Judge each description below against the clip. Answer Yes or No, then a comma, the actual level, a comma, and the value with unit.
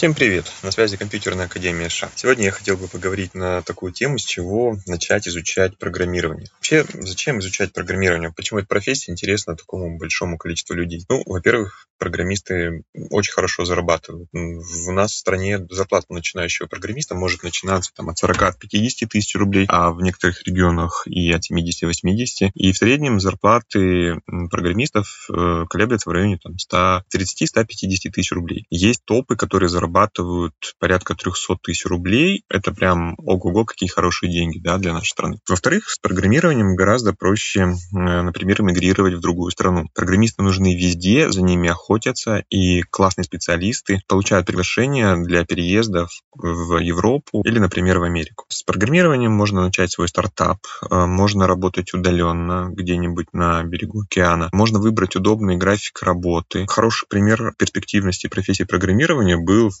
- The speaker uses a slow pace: No, average, 145 wpm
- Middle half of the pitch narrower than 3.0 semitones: Yes, narrow, 2.6 semitones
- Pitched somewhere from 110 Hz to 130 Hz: No, very low, 95 Hz